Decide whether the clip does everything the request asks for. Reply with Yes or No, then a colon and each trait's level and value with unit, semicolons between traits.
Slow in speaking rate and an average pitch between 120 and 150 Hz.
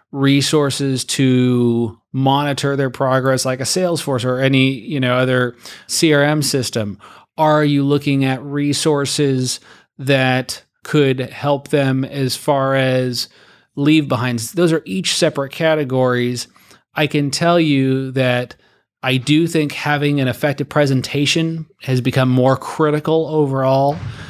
Yes: slow, 125 wpm; low, 135 Hz